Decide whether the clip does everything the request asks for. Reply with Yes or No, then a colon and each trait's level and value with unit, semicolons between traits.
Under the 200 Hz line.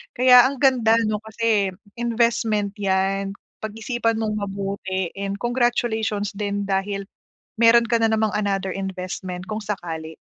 No: high, 210 Hz